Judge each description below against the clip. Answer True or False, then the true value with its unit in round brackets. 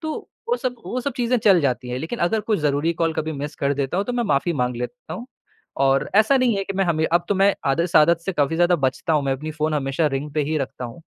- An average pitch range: False (6.2 semitones)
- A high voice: False (160 Hz)